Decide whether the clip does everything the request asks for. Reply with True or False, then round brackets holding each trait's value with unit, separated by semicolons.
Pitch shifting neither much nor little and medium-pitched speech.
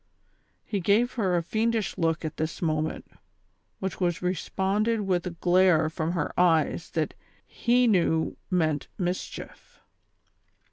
True (3.6 semitones; 180 Hz)